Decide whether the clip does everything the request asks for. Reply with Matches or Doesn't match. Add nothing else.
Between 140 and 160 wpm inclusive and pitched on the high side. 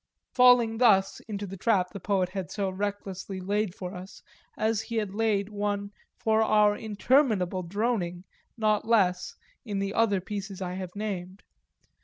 Matches